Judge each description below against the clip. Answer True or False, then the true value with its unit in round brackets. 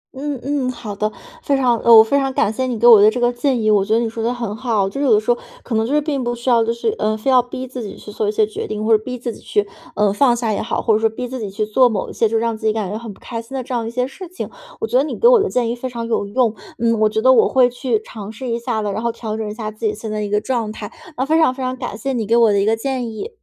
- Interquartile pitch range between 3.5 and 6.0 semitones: False (2.9 semitones)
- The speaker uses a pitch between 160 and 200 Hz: False (230 Hz)